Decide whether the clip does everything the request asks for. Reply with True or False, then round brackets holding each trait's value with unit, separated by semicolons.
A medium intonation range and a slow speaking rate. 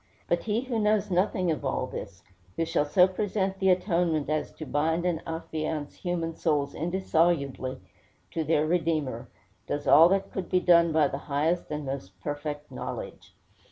False (3.5 semitones; 165 wpm)